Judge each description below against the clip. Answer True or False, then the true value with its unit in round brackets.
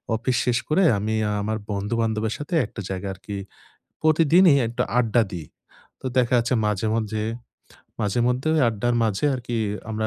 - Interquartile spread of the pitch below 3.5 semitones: True (2.8 semitones)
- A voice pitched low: True (115 Hz)